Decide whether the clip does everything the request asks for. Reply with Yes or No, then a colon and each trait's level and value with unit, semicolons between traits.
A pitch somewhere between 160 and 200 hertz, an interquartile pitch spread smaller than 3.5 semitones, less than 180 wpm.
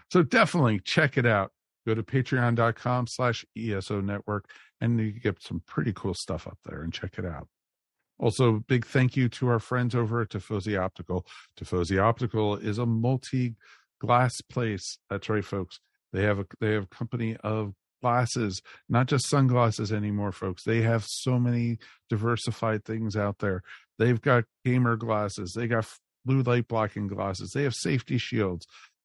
No: low, 115 Hz; average, 3.1 semitones; average, 165 wpm